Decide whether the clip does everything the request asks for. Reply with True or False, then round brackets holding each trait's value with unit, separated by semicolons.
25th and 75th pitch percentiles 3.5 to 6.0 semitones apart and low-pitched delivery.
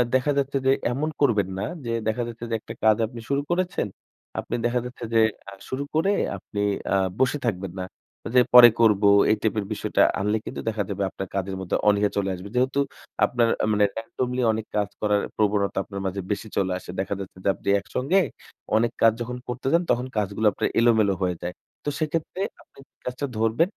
True (3.9 semitones; 110 Hz)